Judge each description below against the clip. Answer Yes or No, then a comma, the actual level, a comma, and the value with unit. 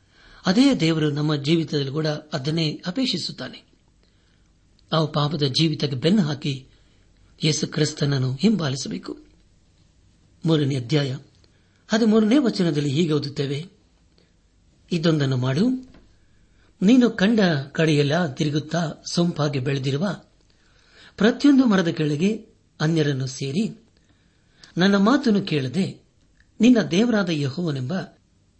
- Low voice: No, medium, 150 Hz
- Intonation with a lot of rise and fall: Yes, wide, 7.3 semitones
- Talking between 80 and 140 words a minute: Yes, average, 85 wpm